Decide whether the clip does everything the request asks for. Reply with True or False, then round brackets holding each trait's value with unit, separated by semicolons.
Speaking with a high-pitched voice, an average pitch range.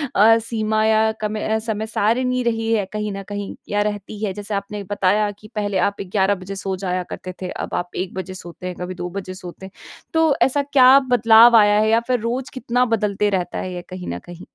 True (205 Hz; 3.0 semitones)